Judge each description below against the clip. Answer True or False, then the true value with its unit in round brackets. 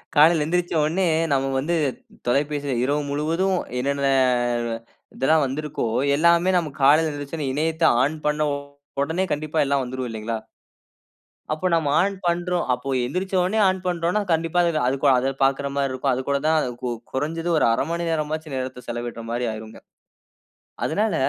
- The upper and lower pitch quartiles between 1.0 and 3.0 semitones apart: False (3.7 semitones)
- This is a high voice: False (150 Hz)